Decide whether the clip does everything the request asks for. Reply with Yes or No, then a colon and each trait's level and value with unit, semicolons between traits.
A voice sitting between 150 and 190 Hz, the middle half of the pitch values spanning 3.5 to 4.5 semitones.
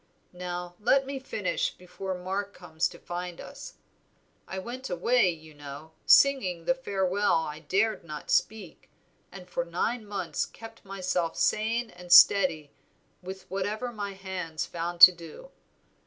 Yes: medium, 185 Hz; average, 3.8 semitones